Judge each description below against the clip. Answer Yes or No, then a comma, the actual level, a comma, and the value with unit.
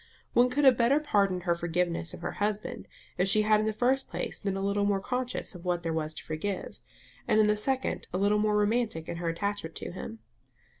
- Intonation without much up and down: No, average, 3.7 semitones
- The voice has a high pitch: Yes, high, 205 Hz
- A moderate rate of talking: No, fast, 230 wpm